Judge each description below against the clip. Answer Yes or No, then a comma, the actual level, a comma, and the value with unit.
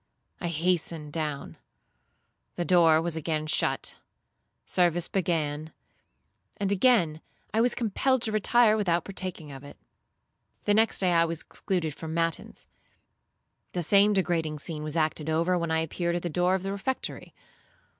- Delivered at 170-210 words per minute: No, average, 150 wpm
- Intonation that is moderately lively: Yes, average, 3.3 semitones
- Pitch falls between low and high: Yes, medium, 170 Hz